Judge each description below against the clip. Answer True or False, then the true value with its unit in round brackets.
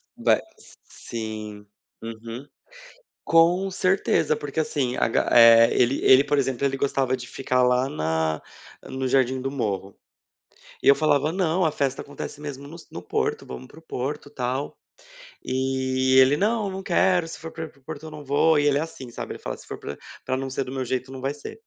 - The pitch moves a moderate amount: True (3.3 semitones)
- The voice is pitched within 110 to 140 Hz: True (135 Hz)